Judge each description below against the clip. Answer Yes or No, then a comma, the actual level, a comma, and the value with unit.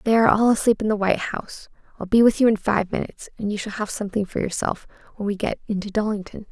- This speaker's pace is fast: Yes, fast, 250 wpm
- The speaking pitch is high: Yes, high, 210 Hz